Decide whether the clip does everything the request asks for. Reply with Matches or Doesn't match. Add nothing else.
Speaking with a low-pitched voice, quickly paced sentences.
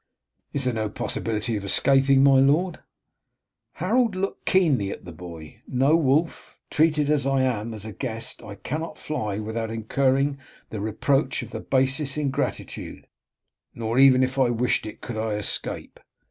Doesn't match